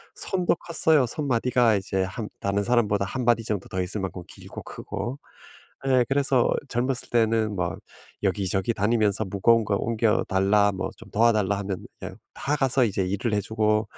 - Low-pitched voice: Yes, low, 110 Hz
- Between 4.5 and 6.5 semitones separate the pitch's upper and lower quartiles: No, average, 3.4 semitones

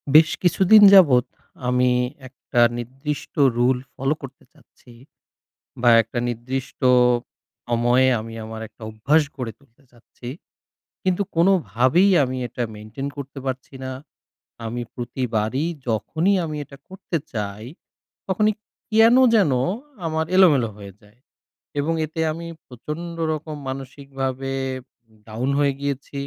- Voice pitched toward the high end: No, low, 135 Hz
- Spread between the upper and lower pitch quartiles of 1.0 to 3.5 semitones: No, average, 4.6 semitones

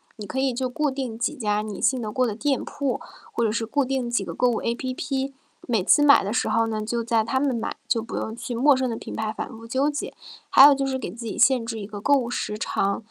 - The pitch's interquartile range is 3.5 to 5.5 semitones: No, average, 3.1 semitones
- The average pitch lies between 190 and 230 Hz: No, high, 240 Hz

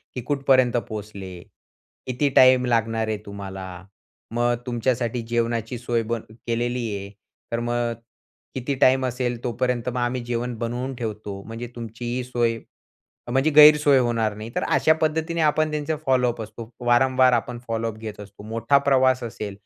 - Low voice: Yes, low, 120 Hz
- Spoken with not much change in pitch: Yes, narrow, 2.2 semitones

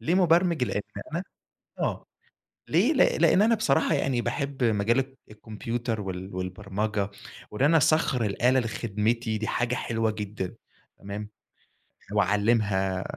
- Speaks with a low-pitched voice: Yes, low, 110 Hz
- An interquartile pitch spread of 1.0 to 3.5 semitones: No, average, 4.3 semitones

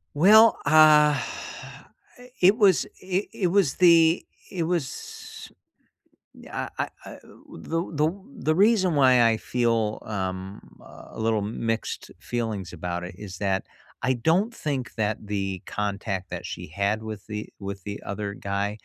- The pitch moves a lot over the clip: Yes, wide, 8.3 semitones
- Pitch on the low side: Yes, low, 115 Hz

